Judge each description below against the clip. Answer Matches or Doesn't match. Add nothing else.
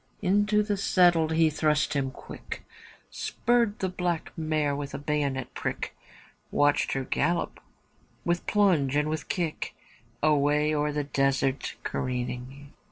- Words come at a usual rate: Doesn't match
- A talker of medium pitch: Matches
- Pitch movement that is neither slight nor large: Matches